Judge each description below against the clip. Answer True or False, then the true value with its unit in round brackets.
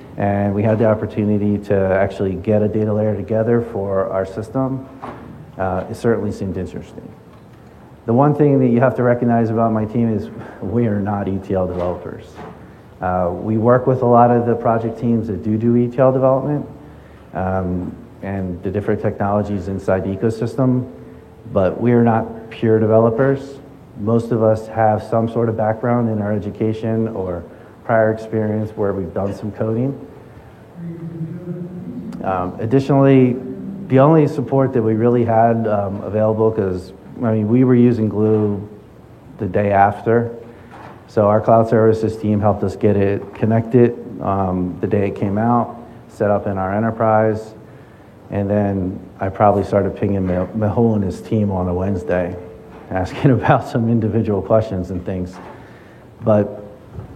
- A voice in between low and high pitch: False (110 Hz)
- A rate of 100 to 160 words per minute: True (155 wpm)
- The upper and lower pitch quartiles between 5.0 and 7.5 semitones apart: False (2.9 semitones)